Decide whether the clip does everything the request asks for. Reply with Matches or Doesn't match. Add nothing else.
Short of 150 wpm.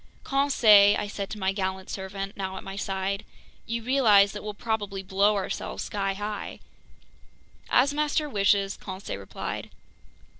Matches